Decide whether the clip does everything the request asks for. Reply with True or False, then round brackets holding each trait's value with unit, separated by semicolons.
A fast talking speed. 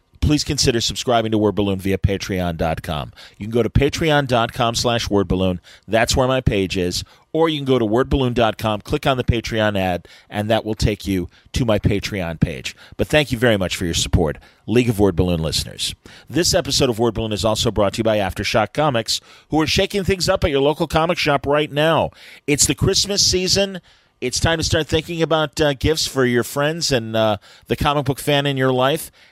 True (210 wpm)